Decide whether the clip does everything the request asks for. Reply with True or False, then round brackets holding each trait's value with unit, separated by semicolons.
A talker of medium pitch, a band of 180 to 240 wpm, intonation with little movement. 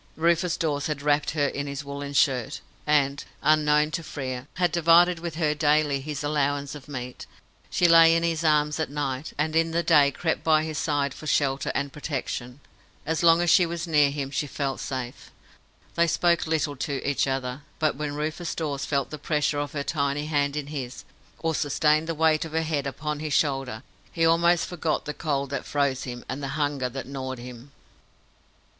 True (150 Hz; 195 wpm; 2.3 semitones)